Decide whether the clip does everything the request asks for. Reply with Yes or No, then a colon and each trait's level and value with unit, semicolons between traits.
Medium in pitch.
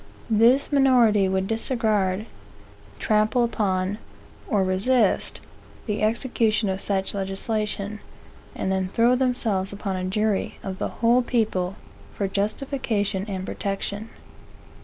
No: high, 210 Hz